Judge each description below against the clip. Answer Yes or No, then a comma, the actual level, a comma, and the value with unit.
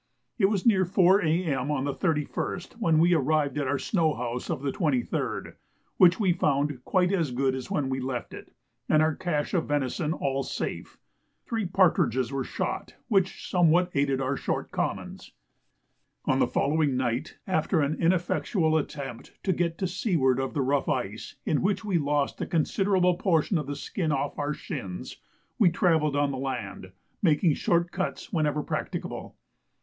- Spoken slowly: No, average, 170 wpm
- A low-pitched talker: No, medium, 155 Hz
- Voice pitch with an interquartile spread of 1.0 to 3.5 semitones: No, average, 4.4 semitones